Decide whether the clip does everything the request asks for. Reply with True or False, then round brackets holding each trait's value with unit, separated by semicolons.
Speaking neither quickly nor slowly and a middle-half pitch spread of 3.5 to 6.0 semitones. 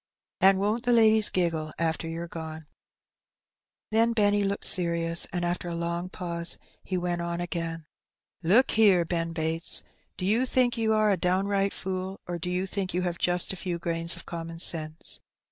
False (195 wpm; 2.9 semitones)